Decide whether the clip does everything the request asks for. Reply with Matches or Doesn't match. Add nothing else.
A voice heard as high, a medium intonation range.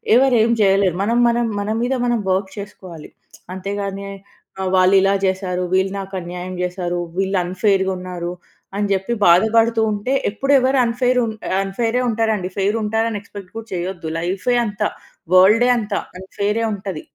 Matches